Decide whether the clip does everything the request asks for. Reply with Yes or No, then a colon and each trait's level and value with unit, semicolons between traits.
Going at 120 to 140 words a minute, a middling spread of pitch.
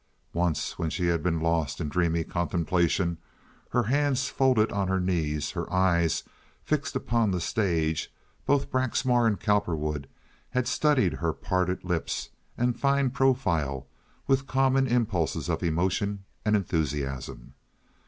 No: slow, 135 wpm; wide, 6.9 semitones